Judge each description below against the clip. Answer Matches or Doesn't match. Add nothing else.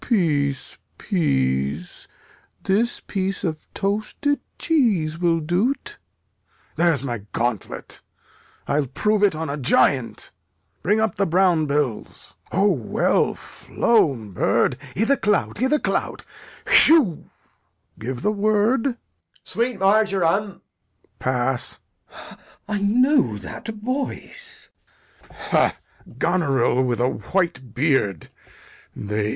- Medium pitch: Matches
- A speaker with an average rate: Doesn't match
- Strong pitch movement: Matches